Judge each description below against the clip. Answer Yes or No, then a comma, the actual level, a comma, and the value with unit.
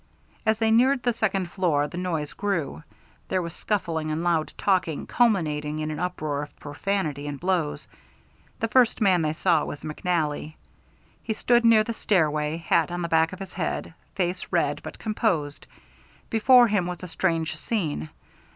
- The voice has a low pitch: No, medium, 175 Hz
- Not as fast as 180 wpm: Yes, average, 170 wpm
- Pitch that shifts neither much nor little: Yes, average, 4.9 semitones